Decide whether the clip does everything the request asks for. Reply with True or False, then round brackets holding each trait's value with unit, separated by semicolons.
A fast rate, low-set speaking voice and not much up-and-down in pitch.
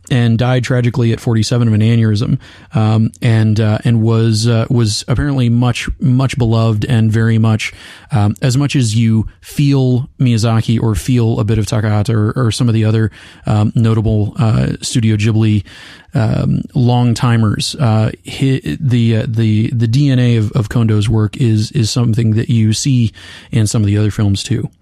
False (175 wpm; 115 Hz; 2.3 semitones)